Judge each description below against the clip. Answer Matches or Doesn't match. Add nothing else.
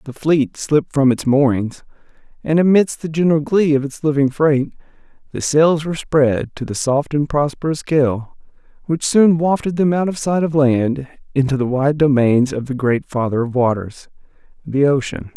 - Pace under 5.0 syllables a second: Matches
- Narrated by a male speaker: Matches